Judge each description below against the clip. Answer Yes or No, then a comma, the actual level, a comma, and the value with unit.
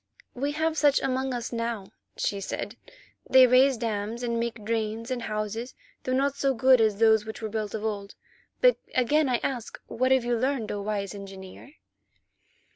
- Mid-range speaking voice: No, high, 235 Hz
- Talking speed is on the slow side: No, average, 175 wpm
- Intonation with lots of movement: No, average, 3.4 semitones